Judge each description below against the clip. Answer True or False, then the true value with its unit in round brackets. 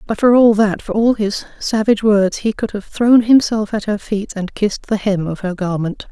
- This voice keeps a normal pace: False (225 wpm)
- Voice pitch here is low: False (210 Hz)